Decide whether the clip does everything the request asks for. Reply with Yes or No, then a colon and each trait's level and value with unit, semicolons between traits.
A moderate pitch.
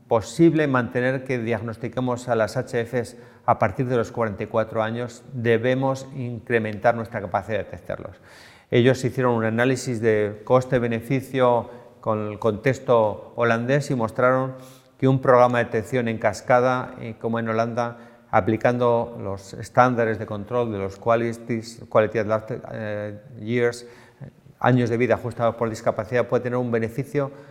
No: low, 120 Hz